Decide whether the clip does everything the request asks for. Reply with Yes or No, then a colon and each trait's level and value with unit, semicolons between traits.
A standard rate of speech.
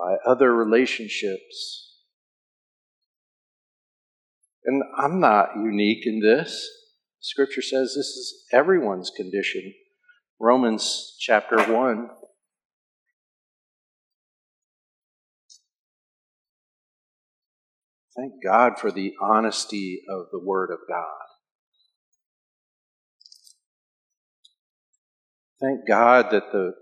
No: slow, 70 wpm